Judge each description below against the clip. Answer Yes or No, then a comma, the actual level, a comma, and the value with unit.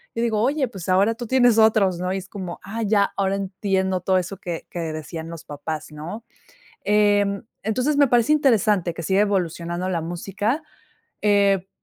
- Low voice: No, high, 195 Hz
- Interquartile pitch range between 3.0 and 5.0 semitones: Yes, average, 3.7 semitones